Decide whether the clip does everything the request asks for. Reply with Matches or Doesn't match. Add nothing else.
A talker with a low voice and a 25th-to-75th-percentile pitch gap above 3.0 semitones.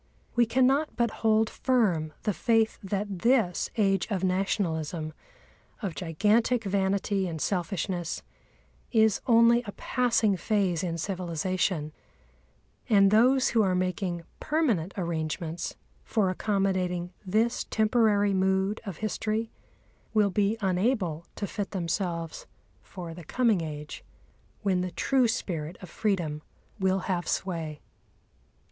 Doesn't match